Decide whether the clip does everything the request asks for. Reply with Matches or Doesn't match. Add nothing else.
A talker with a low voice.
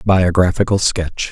Matches